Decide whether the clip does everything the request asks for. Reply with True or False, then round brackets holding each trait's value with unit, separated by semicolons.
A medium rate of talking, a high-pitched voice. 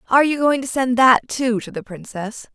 False (235 wpm; 245 Hz)